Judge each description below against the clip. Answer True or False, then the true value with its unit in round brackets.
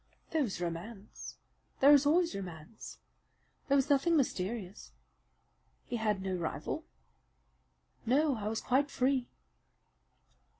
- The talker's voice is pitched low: False (235 Hz)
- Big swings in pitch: True (6.4 semitones)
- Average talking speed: False (115 wpm)